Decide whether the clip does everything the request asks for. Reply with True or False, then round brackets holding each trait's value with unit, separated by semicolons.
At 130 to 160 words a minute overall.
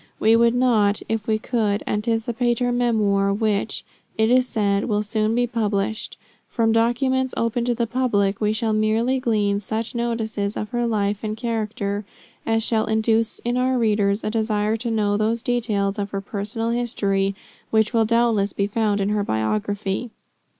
False (170 wpm)